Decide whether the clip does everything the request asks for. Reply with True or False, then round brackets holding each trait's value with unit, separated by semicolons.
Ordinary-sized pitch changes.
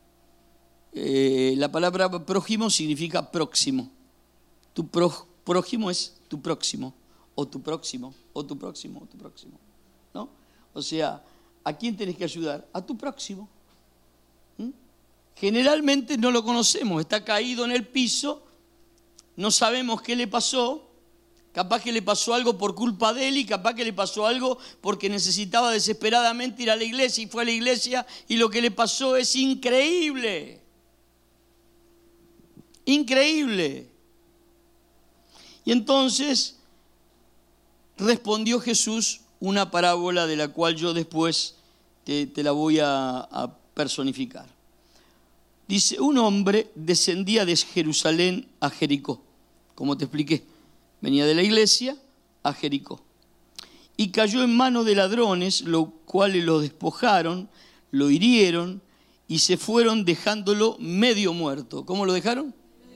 False (6.4 semitones)